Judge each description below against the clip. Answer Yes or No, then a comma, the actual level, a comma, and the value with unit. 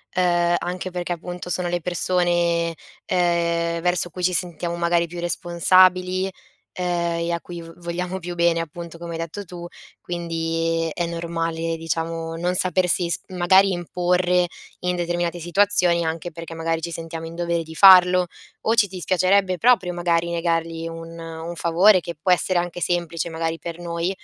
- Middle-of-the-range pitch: Yes, medium, 175 Hz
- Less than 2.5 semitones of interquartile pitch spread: Yes, narrow, 1.2 semitones